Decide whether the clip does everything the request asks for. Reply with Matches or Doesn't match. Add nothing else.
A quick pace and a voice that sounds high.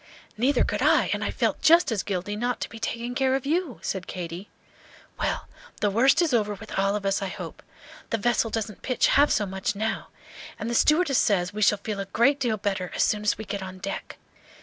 Matches